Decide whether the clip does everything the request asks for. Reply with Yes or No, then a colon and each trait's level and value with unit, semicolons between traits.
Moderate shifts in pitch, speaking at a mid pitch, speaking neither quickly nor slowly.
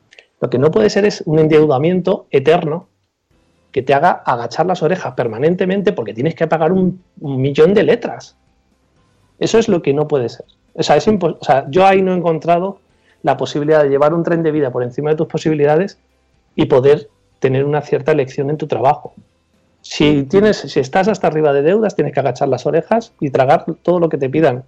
No: average, 4.3 semitones; medium, 155 Hz; fast, 205 wpm